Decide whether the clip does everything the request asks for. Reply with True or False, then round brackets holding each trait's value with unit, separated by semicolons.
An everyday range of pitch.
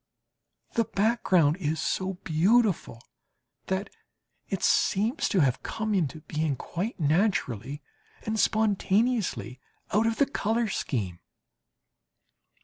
False (6.3 semitones)